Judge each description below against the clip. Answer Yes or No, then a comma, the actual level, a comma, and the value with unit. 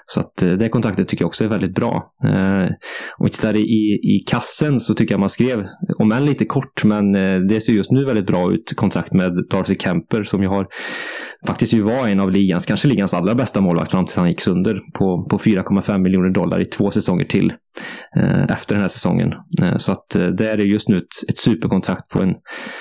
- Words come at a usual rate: No, fast, 210 wpm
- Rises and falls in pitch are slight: Yes, narrow, 2.2 semitones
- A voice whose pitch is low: Yes, low, 105 Hz